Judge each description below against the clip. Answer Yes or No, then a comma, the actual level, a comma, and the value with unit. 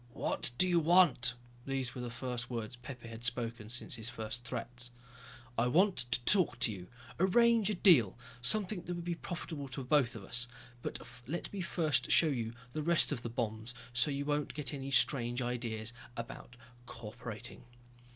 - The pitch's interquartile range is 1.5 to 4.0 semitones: No, wide, 5.5 semitones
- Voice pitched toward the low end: Yes, low, 125 Hz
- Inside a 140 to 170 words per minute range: No, average, 180 wpm